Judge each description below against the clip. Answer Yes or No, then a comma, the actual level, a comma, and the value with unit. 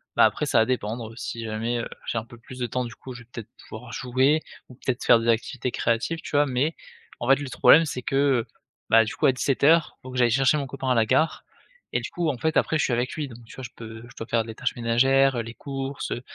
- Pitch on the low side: Yes, low, 125 Hz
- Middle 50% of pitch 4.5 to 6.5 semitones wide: No, average, 2.7 semitones